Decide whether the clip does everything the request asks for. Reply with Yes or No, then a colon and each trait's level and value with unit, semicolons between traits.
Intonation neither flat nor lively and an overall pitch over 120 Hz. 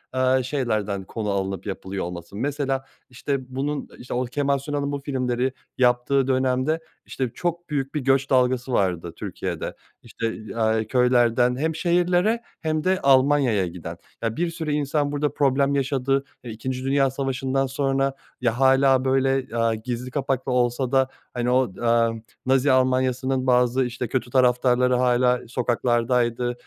No: narrow, 2.1 semitones; low, 130 Hz